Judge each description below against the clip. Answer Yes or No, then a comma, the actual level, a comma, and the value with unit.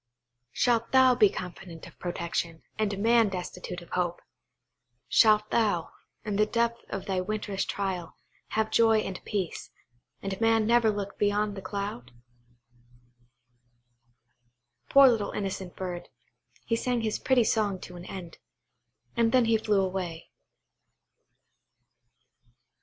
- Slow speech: Yes, slow, 125 wpm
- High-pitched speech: Yes, high, 205 Hz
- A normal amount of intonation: Yes, average, 3.5 semitones